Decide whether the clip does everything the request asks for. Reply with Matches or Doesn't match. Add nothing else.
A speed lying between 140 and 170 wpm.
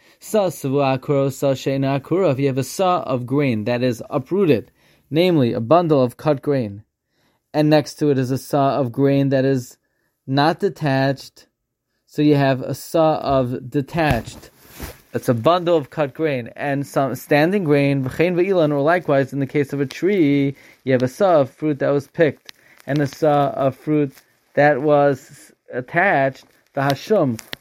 Matches